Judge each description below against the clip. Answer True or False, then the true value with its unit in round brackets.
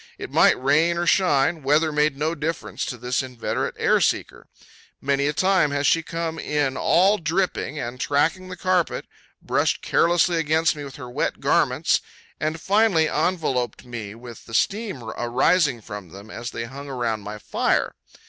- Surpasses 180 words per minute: False (165 wpm)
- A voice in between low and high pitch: True (145 Hz)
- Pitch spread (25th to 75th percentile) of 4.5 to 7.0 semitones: True (5.1 semitones)